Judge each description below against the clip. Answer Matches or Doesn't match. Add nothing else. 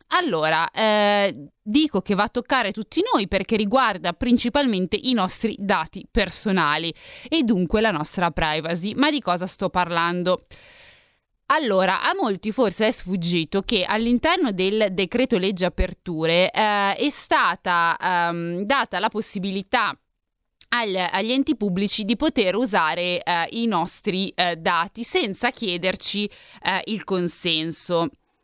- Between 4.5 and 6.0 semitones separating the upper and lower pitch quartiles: Matches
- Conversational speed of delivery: Matches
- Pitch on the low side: Doesn't match